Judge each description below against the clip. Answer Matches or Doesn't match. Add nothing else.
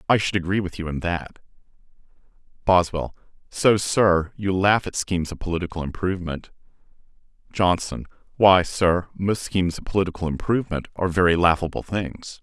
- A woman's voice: Doesn't match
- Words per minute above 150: Doesn't match